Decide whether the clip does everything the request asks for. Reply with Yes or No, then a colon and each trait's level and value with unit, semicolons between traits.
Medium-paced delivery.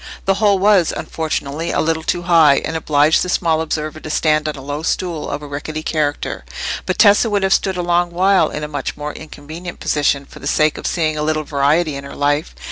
No: fast, 225 wpm